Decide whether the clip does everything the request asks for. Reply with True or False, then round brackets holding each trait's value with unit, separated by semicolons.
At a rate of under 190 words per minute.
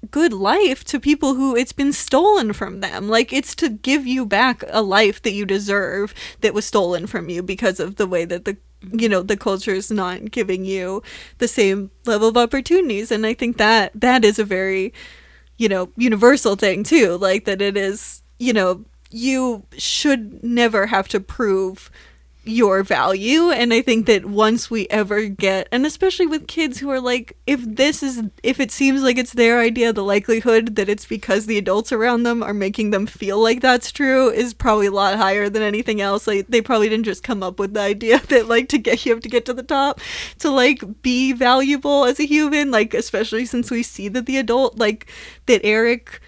False (205 wpm)